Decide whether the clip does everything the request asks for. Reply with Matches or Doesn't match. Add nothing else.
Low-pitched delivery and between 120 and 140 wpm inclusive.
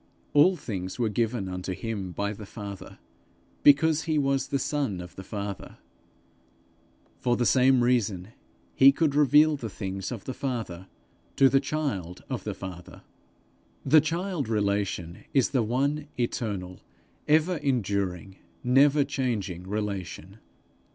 Matches